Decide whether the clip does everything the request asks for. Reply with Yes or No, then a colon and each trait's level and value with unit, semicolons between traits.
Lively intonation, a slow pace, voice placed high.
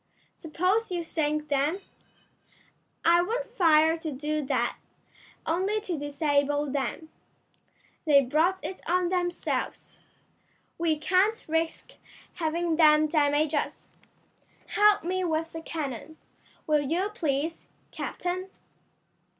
No: average, 3.1 semitones; slow, 110 wpm; very high, 320 Hz